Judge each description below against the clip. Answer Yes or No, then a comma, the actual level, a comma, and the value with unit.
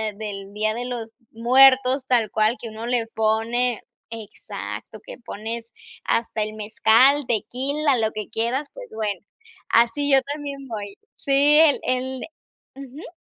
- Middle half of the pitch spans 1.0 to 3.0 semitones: No, average, 3.6 semitones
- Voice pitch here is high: Yes, high, 235 Hz